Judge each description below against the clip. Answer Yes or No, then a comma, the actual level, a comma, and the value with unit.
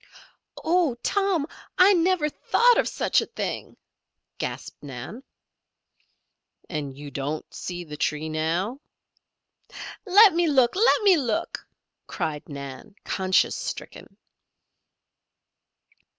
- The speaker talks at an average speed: No, slow, 105 wpm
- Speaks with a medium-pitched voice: No, high, 215 Hz